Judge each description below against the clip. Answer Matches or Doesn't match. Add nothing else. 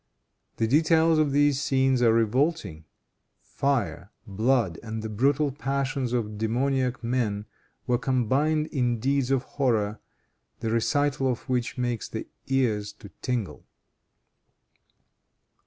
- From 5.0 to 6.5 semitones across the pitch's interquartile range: Doesn't match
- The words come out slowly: Matches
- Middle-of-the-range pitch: Doesn't match